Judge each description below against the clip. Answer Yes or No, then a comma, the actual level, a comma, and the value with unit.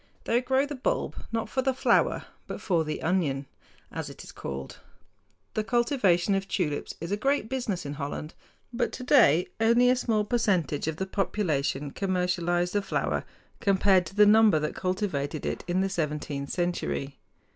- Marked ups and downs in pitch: Yes, wide, 6.2 semitones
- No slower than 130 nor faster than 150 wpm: No, average, 165 wpm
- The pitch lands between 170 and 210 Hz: Yes, high, 190 Hz